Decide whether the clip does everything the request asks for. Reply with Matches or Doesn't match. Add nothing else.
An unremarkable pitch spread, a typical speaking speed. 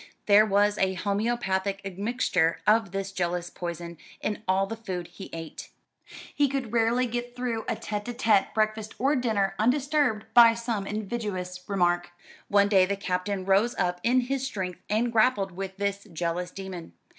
Matches